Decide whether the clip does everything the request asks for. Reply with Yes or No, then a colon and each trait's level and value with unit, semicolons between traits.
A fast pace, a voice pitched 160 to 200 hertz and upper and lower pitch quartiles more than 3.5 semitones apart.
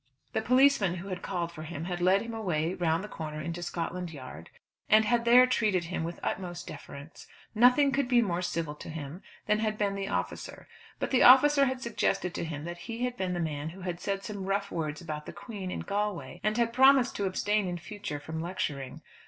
Yes: fast, 220 wpm; medium, 185 Hz; average, 4.8 semitones